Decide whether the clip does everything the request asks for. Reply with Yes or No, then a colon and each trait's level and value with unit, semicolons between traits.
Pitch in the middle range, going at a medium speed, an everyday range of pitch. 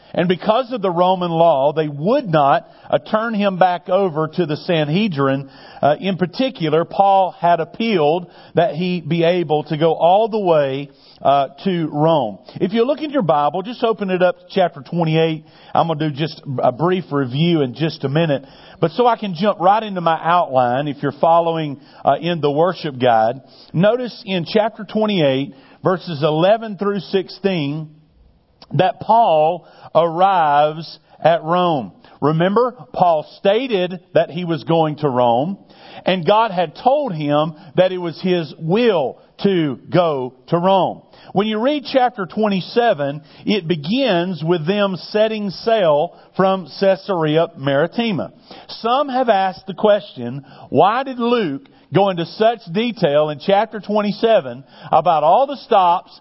Yes: medium, 175 Hz; average, 155 wpm; average, 4.5 semitones